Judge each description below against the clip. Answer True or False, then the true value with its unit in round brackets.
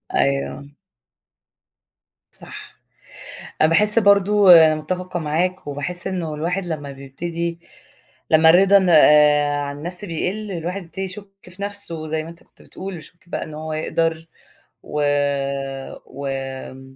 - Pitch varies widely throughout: False (3.3 semitones)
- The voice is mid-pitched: True (165 Hz)